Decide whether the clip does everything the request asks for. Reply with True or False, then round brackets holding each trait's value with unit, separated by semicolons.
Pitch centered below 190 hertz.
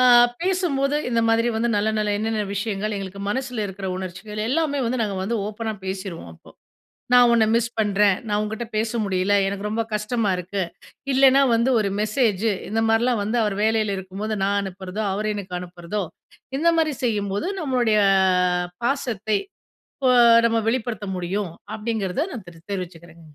False (215 Hz)